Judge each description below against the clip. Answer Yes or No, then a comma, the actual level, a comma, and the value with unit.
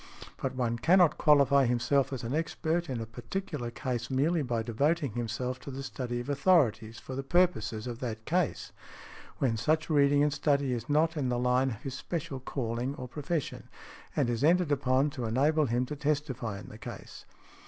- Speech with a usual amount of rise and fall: Yes, average, 3.7 semitones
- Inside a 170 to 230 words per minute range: Yes, average, 185 wpm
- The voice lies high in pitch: No, low, 135 Hz